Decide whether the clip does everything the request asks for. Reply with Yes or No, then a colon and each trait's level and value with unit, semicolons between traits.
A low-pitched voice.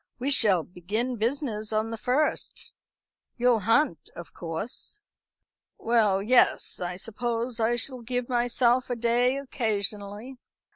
No: high, 235 Hz